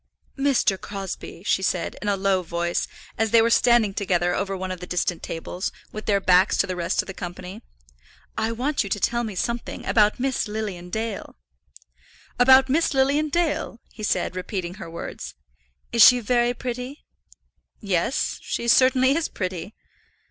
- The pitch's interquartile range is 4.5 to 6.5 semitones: Yes, average, 5.0 semitones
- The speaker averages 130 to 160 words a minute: No, average, 170 wpm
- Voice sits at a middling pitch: No, high, 210 Hz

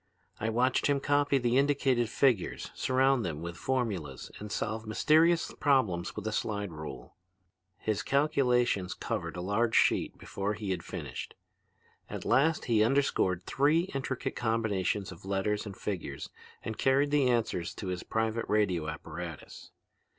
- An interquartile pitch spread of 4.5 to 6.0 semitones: Yes, wide, 5.5 semitones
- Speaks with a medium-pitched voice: No, low, 110 Hz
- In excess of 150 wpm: No, average, 145 wpm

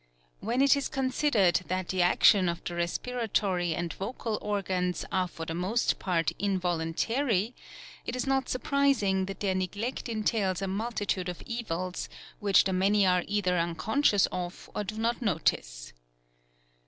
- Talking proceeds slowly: No, average, 150 wpm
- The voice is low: No, high, 195 Hz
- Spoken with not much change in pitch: No, average, 4.1 semitones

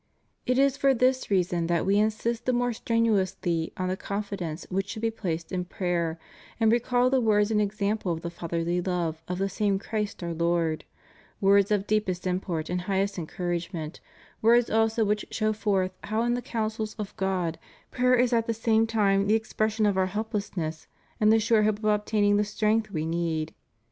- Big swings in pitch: No, average, 3.8 semitones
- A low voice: No, high, 205 Hz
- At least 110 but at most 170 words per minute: No, average, 195 wpm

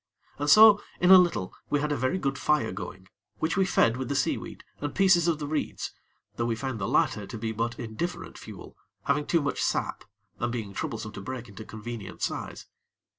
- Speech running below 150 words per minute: No, fast, 205 wpm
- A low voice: Yes, low, 130 Hz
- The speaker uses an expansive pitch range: Yes, wide, 5.8 semitones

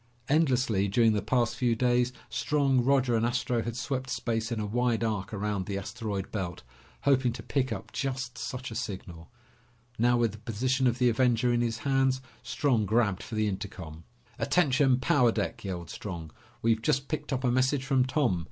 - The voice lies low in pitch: Yes, low, 120 Hz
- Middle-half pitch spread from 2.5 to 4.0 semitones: Yes, average, 3.5 semitones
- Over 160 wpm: Yes, average, 185 wpm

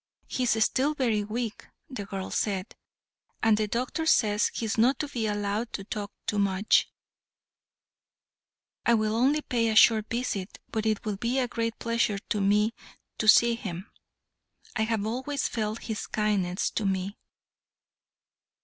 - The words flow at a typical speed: Yes, average, 155 wpm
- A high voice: Yes, high, 220 Hz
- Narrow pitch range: Yes, narrow, 2.3 semitones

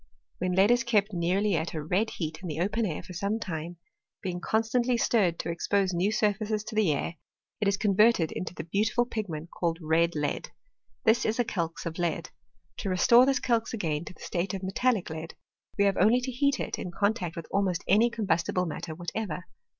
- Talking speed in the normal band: No, fast, 210 wpm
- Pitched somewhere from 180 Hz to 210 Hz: Yes, high, 190 Hz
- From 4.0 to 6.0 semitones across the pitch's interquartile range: Yes, average, 4.5 semitones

